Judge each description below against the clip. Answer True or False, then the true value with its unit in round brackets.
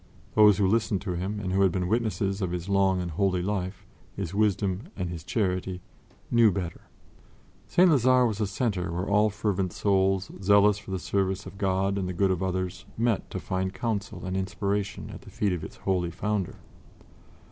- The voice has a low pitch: True (95 Hz)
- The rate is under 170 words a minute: False (190 wpm)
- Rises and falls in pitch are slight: True (2.0 semitones)